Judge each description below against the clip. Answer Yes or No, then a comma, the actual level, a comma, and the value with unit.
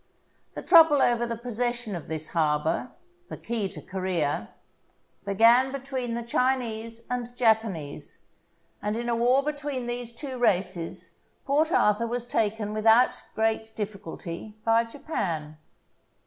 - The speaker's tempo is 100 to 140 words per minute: Yes, slow, 135 wpm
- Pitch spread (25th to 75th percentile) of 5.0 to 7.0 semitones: No, average, 3.7 semitones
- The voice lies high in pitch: Yes, high, 230 Hz